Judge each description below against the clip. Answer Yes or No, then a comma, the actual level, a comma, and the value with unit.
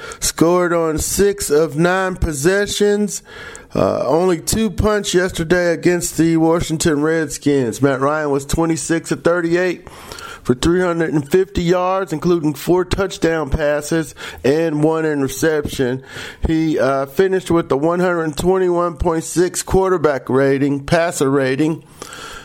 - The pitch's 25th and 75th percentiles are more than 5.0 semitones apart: No, average, 2.8 semitones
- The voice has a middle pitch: Yes, medium, 165 Hz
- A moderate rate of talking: No, slow, 130 wpm